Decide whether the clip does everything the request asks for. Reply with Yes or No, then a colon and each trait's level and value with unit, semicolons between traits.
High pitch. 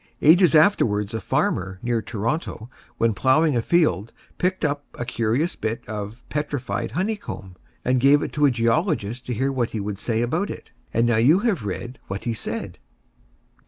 No: low, 120 Hz